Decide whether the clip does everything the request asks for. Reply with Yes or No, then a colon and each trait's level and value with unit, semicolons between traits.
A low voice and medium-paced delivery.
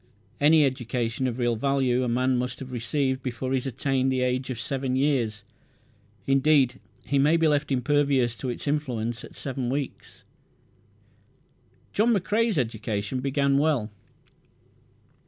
Yes: low, 130 Hz; average, 145 wpm